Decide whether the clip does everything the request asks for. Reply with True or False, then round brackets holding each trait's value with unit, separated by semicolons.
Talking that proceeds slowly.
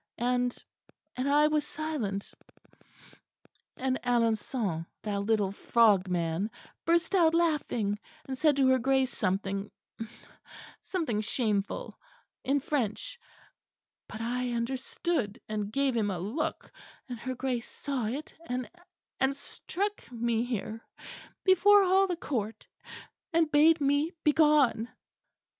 True (115 wpm)